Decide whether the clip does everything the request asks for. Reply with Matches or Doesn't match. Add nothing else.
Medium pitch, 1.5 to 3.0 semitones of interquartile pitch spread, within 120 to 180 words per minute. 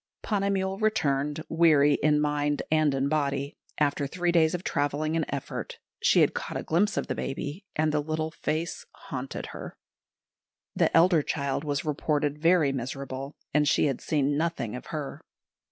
Matches